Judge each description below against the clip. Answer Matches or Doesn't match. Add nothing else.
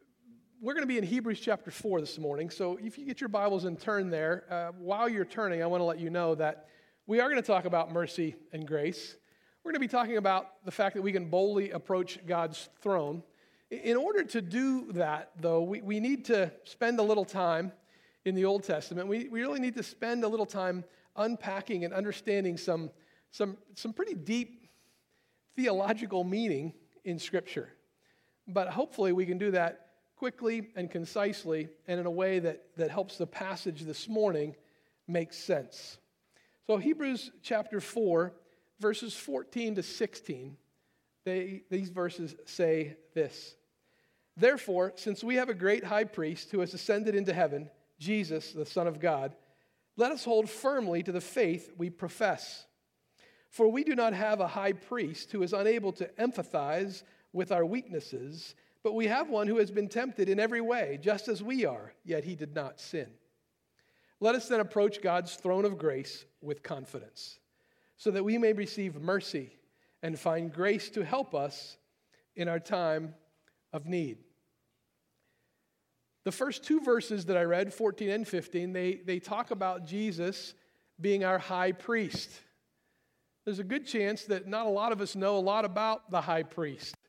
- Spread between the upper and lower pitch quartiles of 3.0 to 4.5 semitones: Matches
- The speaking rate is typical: Matches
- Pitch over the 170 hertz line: Matches